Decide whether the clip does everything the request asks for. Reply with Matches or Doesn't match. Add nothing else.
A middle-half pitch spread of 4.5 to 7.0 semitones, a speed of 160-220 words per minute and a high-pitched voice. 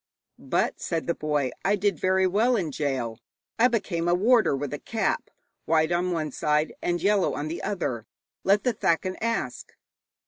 Doesn't match